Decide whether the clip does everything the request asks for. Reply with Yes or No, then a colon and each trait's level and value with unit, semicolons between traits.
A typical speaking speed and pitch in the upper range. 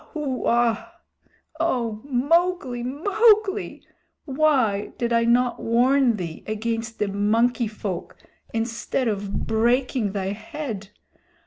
No: slow, 100 wpm; high, 235 Hz